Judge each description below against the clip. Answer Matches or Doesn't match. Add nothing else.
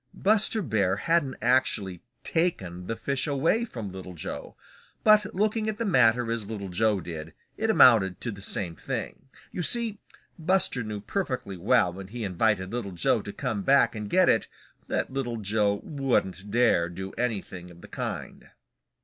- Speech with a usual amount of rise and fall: Doesn't match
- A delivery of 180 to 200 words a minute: Doesn't match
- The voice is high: Doesn't match